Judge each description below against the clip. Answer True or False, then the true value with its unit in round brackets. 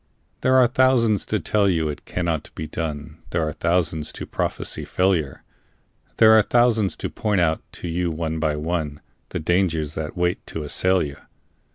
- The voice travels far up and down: False (3.9 semitones)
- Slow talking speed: False (175 wpm)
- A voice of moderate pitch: False (85 Hz)